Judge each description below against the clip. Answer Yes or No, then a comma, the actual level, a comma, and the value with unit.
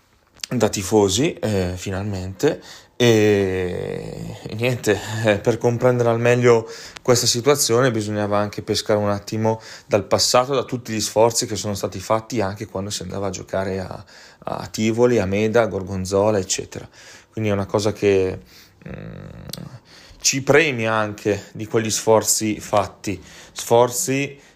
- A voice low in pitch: Yes, low, 110 Hz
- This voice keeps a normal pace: Yes, average, 140 wpm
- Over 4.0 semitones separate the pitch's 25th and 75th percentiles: No, average, 3.0 semitones